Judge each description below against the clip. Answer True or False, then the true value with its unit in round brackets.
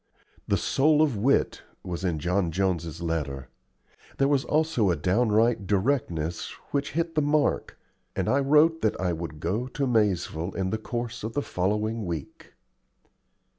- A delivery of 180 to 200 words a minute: False (155 wpm)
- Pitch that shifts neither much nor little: False (7.9 semitones)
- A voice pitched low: True (105 Hz)